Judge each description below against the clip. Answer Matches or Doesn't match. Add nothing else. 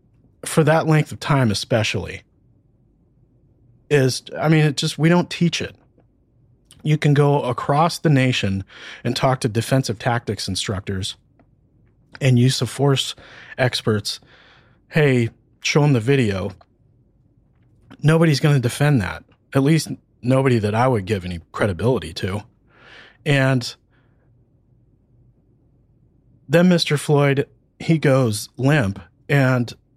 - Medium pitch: Doesn't match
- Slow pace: Matches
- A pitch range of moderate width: Matches